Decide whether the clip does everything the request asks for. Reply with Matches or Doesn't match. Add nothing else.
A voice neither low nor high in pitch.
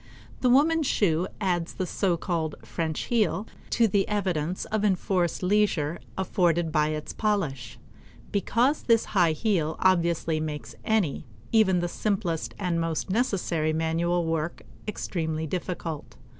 Matches